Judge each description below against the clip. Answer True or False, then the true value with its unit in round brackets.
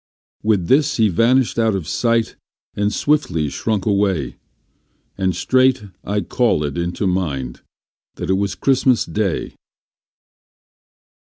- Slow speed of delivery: True (115 wpm)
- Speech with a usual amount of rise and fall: True (4.9 semitones)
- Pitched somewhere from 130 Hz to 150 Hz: False (105 Hz)